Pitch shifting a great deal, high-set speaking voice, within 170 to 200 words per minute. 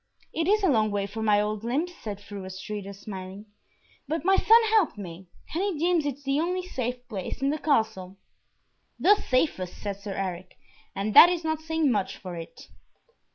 Yes: wide, 8.4 semitones; high, 225 Hz; average, 190 wpm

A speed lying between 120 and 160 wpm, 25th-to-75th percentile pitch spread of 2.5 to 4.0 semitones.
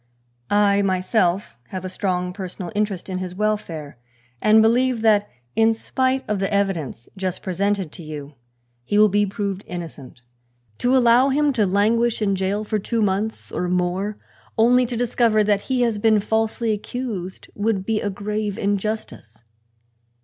Yes: average, 155 wpm; average, 3.0 semitones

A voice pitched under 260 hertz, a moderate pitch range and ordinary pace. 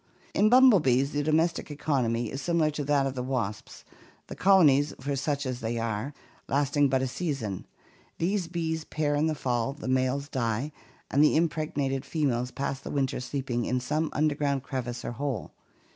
Yes: medium, 140 Hz; average, 3.1 semitones; average, 170 wpm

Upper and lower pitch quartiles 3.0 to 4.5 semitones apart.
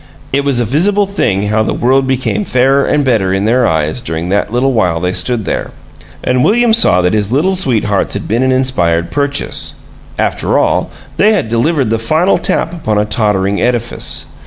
No: wide, 5.4 semitones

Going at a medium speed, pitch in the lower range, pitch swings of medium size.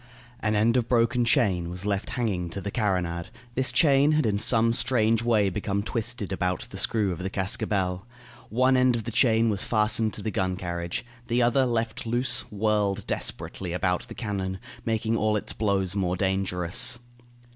Yes: average, 180 wpm; low, 105 Hz; average, 3.6 semitones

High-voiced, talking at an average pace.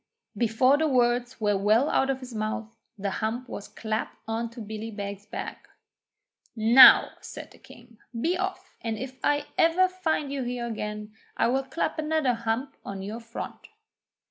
Yes: high, 235 Hz; average, 170 wpm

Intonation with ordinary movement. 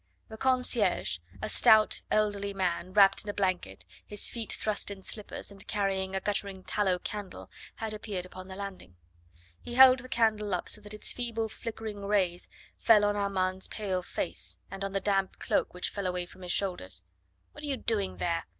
No: narrow, 2.3 semitones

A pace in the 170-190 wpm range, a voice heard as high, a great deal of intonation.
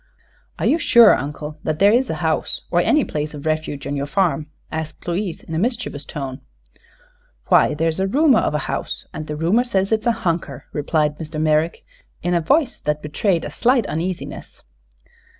No: average, 185 wpm; medium, 165 Hz; wide, 5.8 semitones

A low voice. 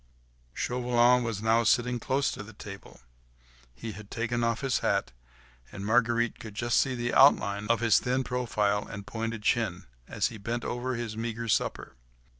Yes: low, 115 Hz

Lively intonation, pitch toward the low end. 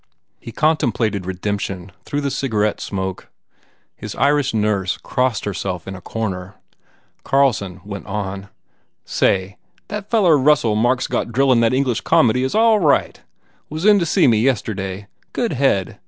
Yes: wide, 5.9 semitones; low, 115 Hz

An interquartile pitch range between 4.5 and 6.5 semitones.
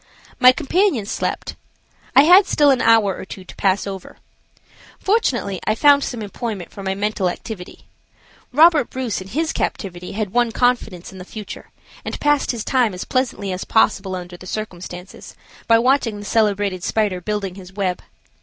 Yes: average, 4.8 semitones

